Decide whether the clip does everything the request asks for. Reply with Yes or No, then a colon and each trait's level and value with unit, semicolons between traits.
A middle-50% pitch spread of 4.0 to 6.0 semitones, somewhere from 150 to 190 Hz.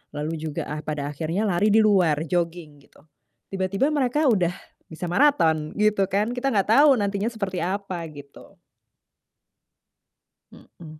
Yes: average, 5.0 semitones; medium, 185 Hz